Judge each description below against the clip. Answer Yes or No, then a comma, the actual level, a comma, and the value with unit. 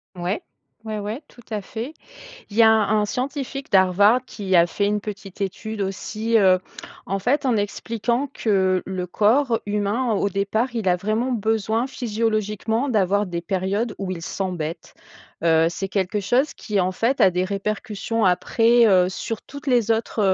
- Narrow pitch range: No, average, 3.2 semitones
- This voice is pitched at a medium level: No, high, 210 Hz